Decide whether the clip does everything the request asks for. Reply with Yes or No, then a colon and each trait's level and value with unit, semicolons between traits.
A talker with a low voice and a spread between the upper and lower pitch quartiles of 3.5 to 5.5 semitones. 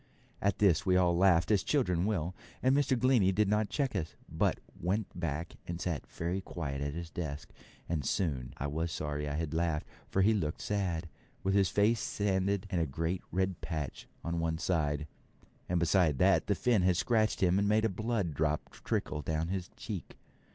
Yes: very low, 90 Hz; average, 3.9 semitones